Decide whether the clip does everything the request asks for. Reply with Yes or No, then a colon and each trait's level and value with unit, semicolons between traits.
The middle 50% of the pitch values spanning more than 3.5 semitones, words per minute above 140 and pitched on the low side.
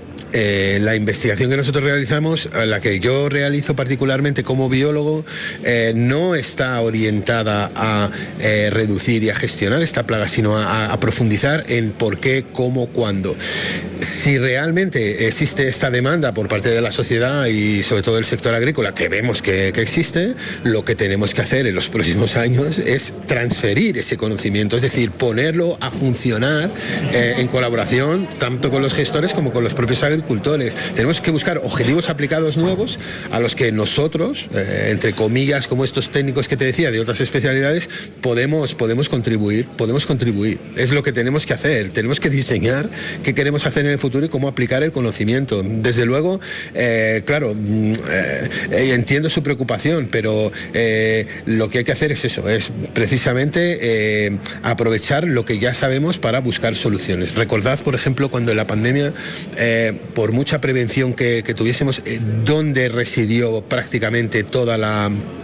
Yes: average, 4.3 semitones; average, 165 wpm; low, 125 Hz